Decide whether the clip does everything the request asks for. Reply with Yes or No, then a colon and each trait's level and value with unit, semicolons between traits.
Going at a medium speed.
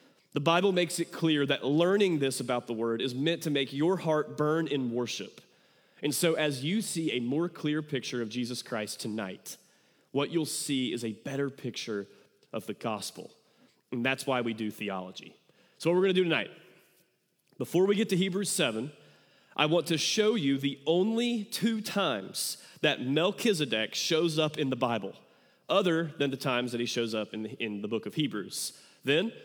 Yes: average, 190 wpm